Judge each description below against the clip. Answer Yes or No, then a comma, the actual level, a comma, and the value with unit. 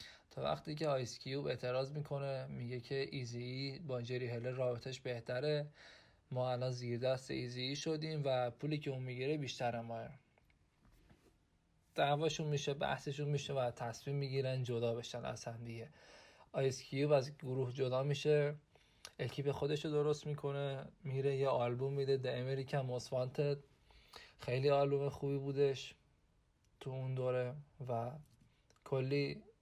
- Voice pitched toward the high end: No, low, 135 Hz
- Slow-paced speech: No, average, 140 wpm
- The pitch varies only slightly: Yes, narrow, 2.2 semitones